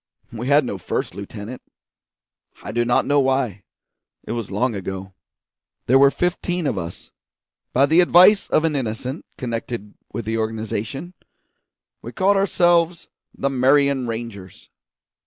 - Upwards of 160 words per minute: No, average, 140 wpm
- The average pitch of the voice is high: No, low, 125 Hz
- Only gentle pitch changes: No, average, 5.0 semitones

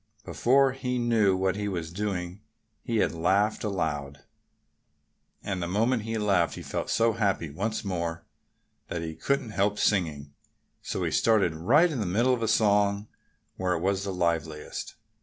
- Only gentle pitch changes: No, average, 4.5 semitones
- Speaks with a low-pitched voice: Yes, low, 100 Hz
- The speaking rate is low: No, average, 165 wpm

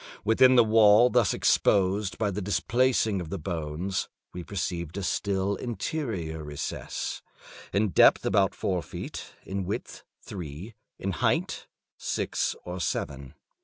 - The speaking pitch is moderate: No, very low, 95 Hz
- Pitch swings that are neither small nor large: Yes, average, 3.7 semitones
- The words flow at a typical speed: No, slow, 130 wpm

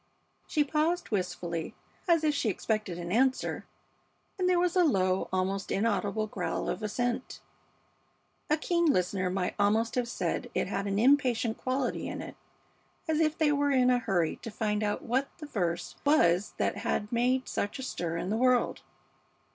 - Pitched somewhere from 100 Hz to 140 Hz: No, high, 230 Hz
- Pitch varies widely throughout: Yes, wide, 6.3 semitones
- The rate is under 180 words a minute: Yes, average, 170 wpm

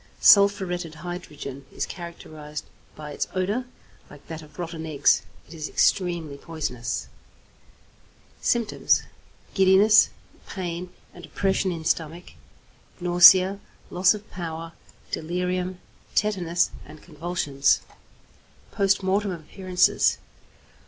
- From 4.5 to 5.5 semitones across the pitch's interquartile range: No, average, 3.1 semitones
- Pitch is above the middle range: No, medium, 175 Hz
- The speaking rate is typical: No, slow, 100 wpm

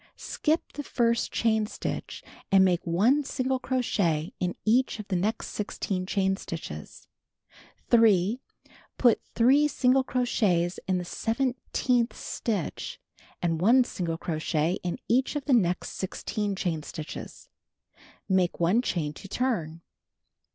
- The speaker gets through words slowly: Yes, slow, 130 wpm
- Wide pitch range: Yes, wide, 6.0 semitones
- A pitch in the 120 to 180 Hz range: No, high, 205 Hz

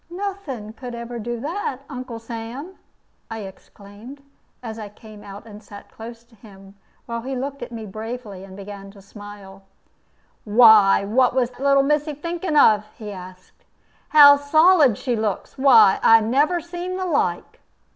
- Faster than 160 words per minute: No, average, 155 wpm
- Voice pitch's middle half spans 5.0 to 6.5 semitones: Yes, average, 5.3 semitones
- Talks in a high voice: Yes, high, 230 Hz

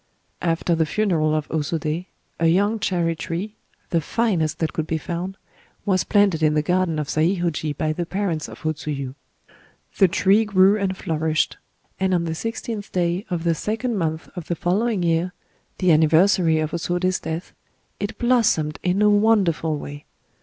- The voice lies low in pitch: No, medium, 170 Hz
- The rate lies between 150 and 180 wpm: Yes, average, 160 wpm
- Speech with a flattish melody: No, average, 3.6 semitones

